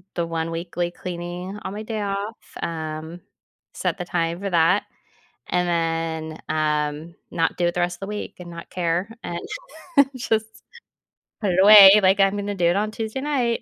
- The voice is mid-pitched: Yes, medium, 175 Hz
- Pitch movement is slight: No, average, 3.5 semitones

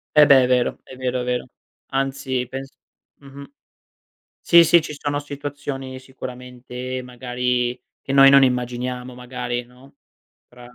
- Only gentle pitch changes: Yes, narrow, 1.7 semitones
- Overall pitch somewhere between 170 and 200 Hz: No, low, 130 Hz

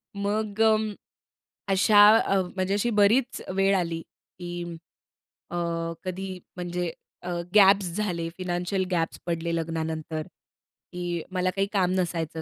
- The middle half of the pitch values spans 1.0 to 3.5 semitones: Yes, narrow, 2.5 semitones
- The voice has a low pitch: No, medium, 180 Hz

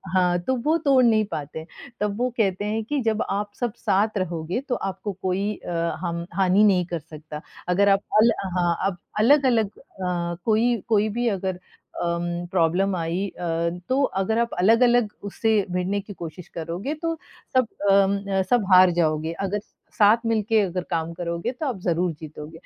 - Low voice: No, high, 195 Hz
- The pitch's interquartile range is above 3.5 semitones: Yes, average, 4.3 semitones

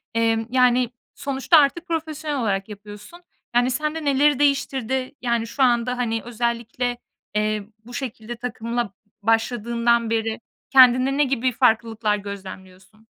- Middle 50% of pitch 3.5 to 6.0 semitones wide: No, average, 2.9 semitones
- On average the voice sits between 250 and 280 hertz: No, high, 240 Hz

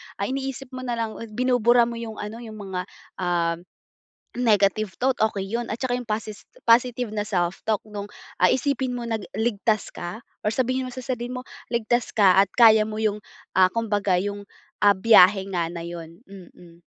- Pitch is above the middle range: Yes, high, 215 Hz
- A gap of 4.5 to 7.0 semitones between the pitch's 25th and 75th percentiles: No, average, 3.5 semitones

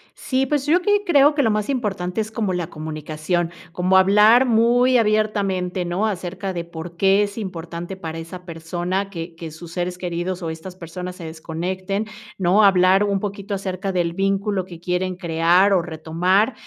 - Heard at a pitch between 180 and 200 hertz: Yes, medium, 185 Hz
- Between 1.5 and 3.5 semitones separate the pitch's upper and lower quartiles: Yes, average, 3.1 semitones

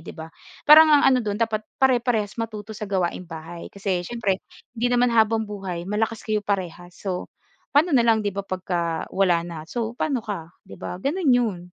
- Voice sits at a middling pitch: No, high, 210 Hz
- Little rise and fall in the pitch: No, average, 4.6 semitones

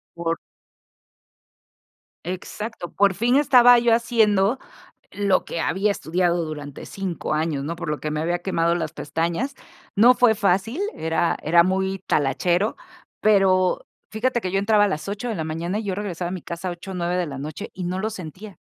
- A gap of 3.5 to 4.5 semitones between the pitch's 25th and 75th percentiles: Yes, average, 3.9 semitones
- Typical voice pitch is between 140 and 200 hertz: Yes, medium, 185 Hz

